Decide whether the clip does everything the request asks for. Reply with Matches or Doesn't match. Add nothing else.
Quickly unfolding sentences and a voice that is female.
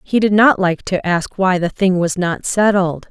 Matches